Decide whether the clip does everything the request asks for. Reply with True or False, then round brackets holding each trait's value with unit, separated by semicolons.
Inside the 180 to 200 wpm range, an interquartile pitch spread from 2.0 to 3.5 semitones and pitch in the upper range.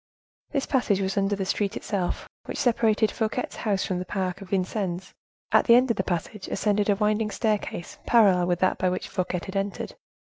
True (195 wpm; 2.5 semitones; 200 Hz)